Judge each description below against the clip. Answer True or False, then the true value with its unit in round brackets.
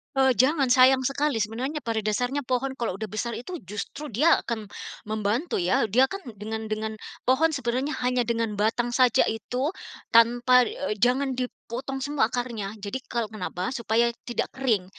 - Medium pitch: False (240 Hz)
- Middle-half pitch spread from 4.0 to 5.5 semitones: False (3.3 semitones)